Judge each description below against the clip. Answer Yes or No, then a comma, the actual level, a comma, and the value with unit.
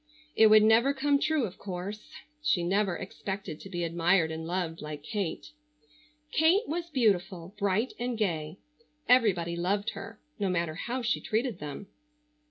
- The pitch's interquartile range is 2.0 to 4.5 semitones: No, wide, 5.4 semitones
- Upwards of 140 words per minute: Yes, average, 155 wpm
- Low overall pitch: No, high, 200 Hz